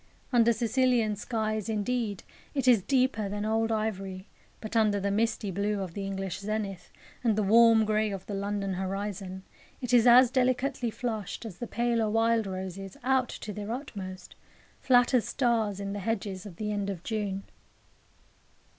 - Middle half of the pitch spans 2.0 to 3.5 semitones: Yes, average, 2.8 semitones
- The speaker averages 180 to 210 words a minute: No, average, 165 wpm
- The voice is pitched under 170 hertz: No, high, 215 Hz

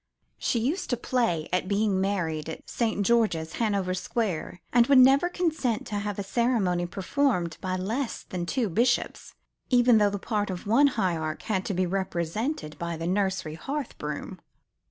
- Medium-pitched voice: No, high, 205 Hz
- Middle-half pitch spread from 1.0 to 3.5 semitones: No, average, 5.0 semitones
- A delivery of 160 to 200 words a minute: Yes, average, 170 wpm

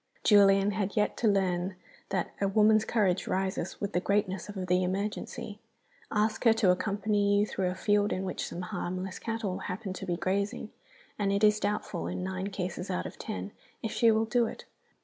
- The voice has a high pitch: Yes, high, 200 Hz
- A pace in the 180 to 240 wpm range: Yes, average, 190 wpm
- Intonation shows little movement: Yes, narrow, 2.2 semitones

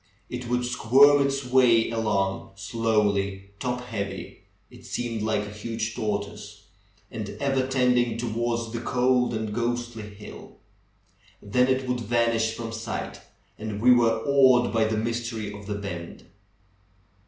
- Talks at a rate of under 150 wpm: Yes, average, 140 wpm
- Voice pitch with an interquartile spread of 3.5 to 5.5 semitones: No, average, 2.7 semitones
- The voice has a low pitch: Yes, low, 115 Hz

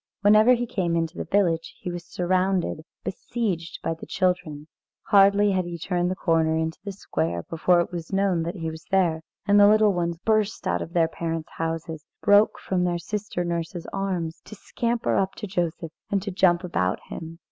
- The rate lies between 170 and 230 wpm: Yes, average, 190 wpm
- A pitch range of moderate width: Yes, average, 3.3 semitones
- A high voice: No, medium, 175 Hz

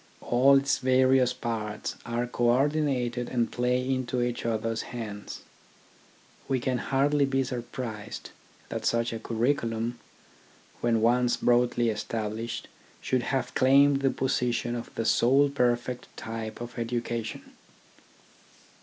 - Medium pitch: No, low, 120 Hz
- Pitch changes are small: Yes, narrow, 1.9 semitones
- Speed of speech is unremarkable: No, slow, 120 wpm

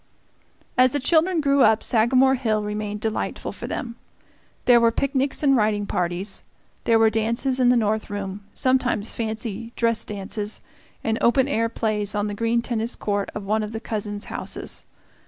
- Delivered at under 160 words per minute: No, average, 170 wpm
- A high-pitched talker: Yes, high, 225 Hz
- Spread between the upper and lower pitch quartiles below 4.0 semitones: Yes, average, 3.0 semitones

